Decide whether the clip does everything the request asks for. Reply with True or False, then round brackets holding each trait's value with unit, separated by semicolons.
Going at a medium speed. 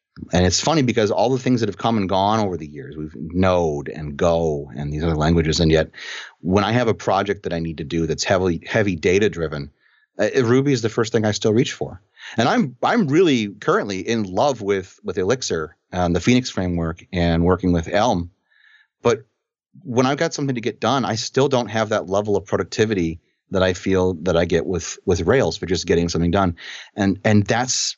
False (210 wpm)